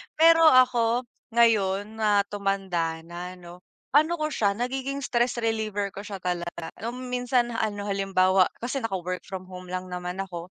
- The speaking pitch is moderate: No, high, 205 Hz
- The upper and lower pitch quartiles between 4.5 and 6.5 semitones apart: Yes, average, 4.8 semitones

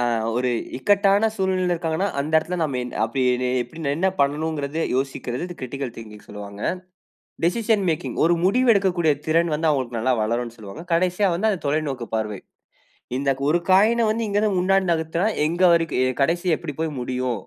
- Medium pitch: Yes, medium, 160 Hz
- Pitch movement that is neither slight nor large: No, wide, 6.4 semitones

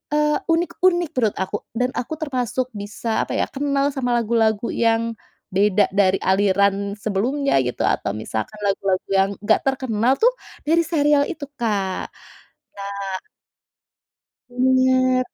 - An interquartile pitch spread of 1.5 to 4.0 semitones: No, average, 5.3 semitones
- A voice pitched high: Yes, high, 230 Hz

